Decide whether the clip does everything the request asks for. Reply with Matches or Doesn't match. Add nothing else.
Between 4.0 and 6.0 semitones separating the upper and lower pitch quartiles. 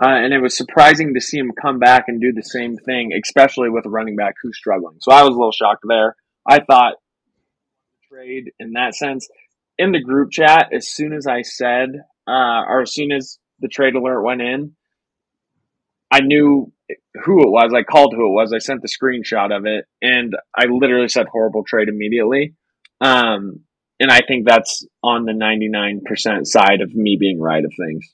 Doesn't match